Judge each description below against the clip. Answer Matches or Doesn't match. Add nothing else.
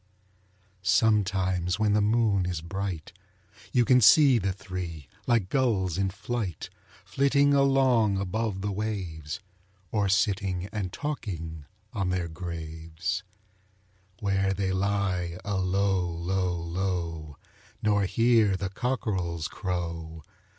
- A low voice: Matches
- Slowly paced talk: Matches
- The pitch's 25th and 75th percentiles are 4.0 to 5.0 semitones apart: Doesn't match